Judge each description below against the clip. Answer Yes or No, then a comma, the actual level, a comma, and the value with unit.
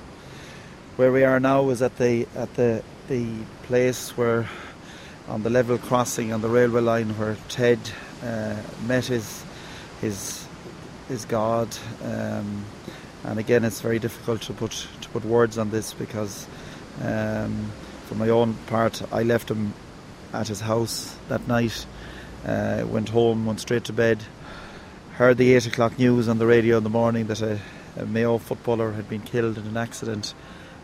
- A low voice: Yes, low, 115 Hz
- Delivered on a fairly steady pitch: Yes, narrow, 1.8 semitones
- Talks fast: No, average, 165 wpm